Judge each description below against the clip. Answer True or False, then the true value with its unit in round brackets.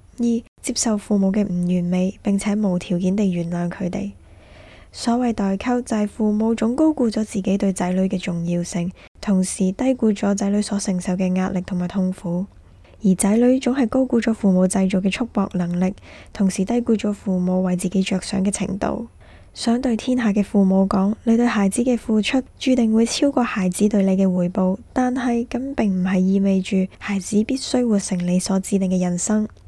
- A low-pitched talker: False (200 Hz)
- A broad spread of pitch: False (3.5 semitones)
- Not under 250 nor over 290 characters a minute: True (280 characters per minute)